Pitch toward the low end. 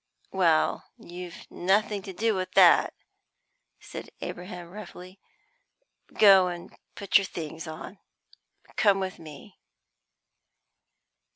No: medium, 185 Hz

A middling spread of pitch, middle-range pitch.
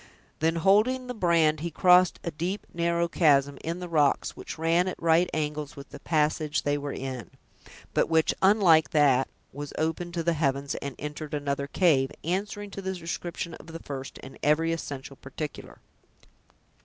Yes: average, 3.1 semitones; medium, 160 Hz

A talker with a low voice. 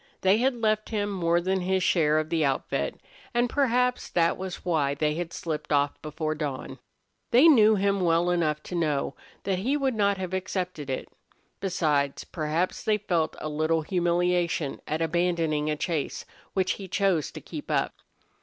No: medium, 175 Hz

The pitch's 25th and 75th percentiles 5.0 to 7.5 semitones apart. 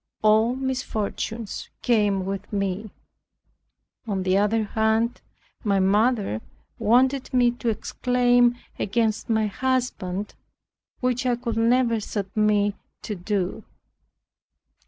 No: average, 3.2 semitones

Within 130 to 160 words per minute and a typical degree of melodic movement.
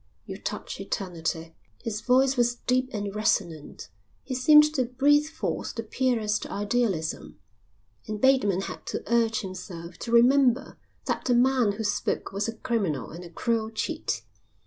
Yes: average, 150 wpm; average, 4.5 semitones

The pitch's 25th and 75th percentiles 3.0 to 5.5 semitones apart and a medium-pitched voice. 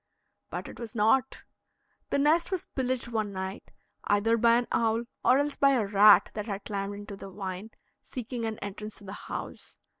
No: average, 3.4 semitones; high, 220 Hz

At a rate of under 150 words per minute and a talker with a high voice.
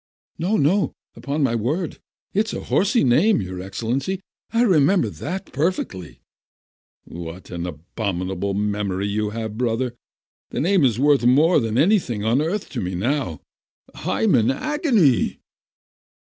No: slow, 135 wpm; low, 125 Hz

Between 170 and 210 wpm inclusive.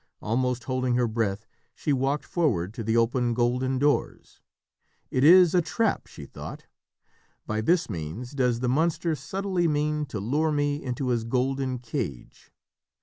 No: average, 150 wpm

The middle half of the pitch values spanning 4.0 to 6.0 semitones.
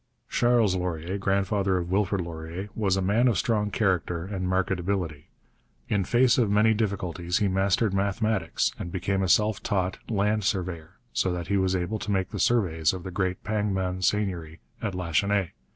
No: narrow, 2.5 semitones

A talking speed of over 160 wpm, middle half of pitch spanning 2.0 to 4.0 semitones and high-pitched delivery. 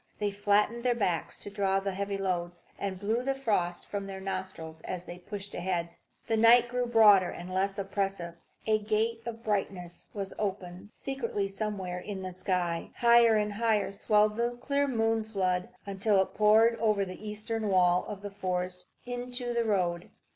Yes: average, 170 wpm; average, 3.2 semitones; high, 200 Hz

